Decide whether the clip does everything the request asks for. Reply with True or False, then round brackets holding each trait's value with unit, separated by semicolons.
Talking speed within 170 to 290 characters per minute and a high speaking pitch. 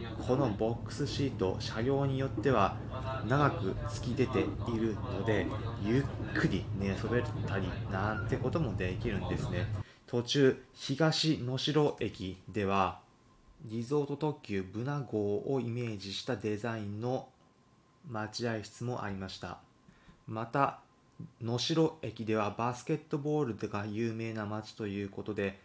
False (265 characters per minute; 115 Hz)